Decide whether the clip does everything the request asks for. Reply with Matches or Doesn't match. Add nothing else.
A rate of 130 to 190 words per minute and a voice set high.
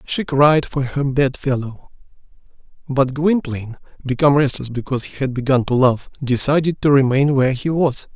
Doesn't match